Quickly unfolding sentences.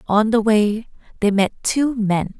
No: average, 175 wpm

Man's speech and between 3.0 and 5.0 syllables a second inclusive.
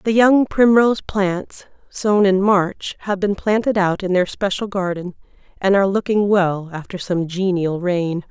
No: female; 4.3 syllables/s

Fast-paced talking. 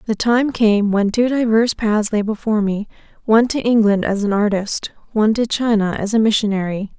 No: average, 180 wpm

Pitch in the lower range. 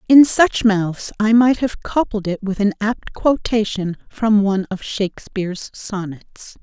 No: high, 210 Hz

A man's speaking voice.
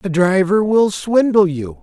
Yes: male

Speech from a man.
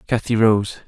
Yes: male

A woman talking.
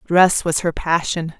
Yes: female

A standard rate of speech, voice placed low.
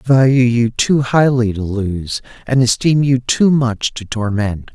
Yes: average, 175 wpm; low, 120 Hz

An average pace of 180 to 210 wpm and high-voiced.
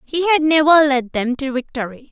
Yes: average, 200 wpm; very high, 280 Hz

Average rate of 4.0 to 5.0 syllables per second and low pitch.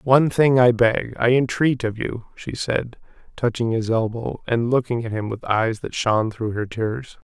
Yes: 4.5 syllables/s; low, 120 Hz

